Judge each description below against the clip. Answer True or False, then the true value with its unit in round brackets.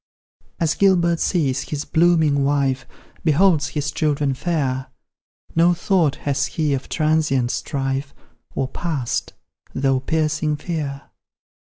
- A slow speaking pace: True (115 wpm)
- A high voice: False (150 Hz)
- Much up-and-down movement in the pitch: False (3.1 semitones)